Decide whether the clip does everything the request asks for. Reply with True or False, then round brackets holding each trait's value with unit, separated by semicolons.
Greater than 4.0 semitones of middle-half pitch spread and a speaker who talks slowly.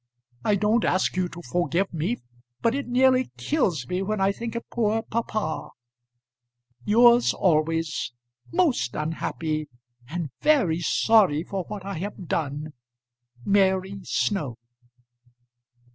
True (5.6 semitones; 120 wpm)